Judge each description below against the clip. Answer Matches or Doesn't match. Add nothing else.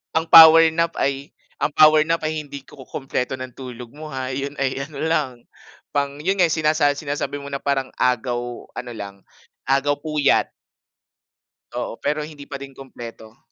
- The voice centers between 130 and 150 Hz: Matches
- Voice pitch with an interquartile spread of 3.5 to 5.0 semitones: Doesn't match